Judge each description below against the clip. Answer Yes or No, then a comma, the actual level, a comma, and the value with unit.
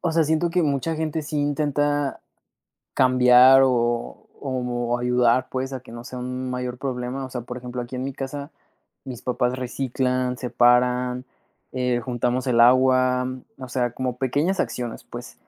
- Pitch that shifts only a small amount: Yes, narrow, 1.6 semitones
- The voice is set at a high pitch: No, low, 125 Hz